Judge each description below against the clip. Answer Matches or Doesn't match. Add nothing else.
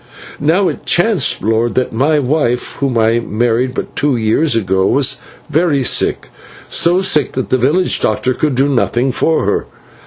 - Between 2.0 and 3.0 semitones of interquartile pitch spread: Doesn't match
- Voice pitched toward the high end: Doesn't match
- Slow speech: Doesn't match